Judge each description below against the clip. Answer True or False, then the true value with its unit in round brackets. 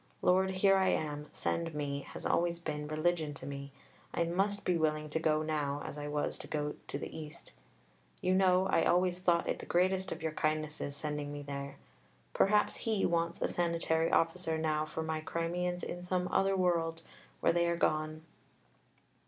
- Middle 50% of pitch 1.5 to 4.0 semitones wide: True (2.8 semitones)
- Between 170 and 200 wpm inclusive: True (185 wpm)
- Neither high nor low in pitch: True (165 Hz)